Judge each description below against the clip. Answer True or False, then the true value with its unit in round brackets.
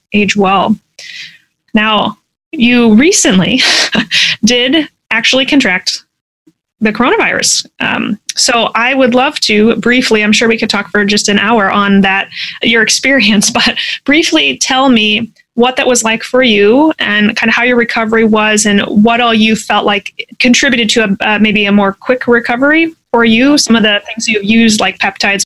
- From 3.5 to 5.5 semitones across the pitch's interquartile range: False (3.0 semitones)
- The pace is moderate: True (170 wpm)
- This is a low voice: False (230 Hz)